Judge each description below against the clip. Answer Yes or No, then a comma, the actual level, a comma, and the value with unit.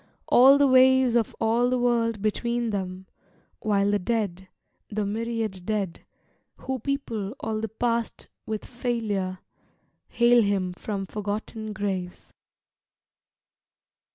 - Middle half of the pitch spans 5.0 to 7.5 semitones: No, average, 3.0 semitones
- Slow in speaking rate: Yes, slow, 115 wpm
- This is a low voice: No, high, 220 Hz